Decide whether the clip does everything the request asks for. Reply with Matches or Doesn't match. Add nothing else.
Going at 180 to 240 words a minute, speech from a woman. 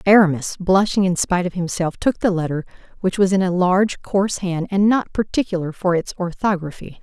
Matches